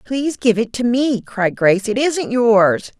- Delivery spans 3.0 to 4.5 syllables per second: Yes, 4.2 syllables/s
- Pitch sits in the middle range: No, high, 235 Hz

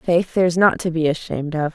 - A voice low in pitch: No, medium, 165 Hz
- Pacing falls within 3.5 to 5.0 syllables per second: No, 5.7 syllables/s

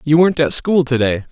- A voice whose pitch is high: No, medium, 145 Hz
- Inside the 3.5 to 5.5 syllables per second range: No, 6.0 syllables/s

